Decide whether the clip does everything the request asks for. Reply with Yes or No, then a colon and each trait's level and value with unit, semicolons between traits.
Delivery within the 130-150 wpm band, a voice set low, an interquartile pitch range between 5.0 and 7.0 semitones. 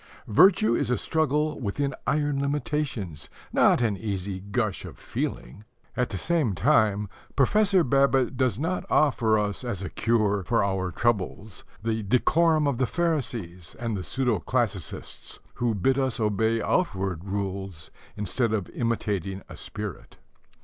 Yes: average, 140 wpm; low, 115 Hz; wide, 5.5 semitones